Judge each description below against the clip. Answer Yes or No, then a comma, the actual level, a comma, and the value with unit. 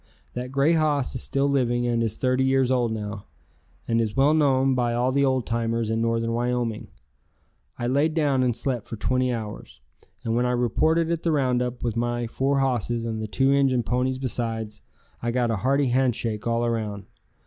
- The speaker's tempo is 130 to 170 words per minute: No, average, 190 wpm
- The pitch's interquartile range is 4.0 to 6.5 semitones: No, narrow, 2.5 semitones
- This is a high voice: No, low, 125 Hz